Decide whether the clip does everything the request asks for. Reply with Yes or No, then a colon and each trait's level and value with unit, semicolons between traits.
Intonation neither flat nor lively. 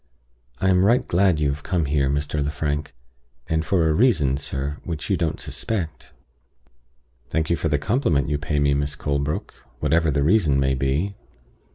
Yes: average, 3.4 semitones